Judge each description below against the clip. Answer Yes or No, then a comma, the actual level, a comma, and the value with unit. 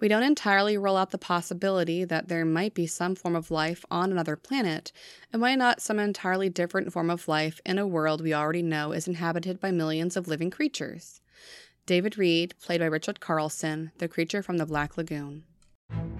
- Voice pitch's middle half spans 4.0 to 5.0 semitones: No, average, 3.3 semitones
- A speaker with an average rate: Yes, average, 195 wpm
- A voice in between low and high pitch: Yes, medium, 175 Hz